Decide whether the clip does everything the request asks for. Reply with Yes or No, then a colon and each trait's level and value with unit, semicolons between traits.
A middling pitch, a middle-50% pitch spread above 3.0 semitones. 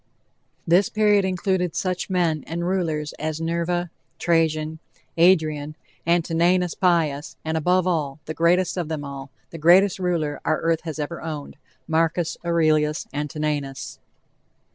No: medium, 165 Hz; narrow, 2.6 semitones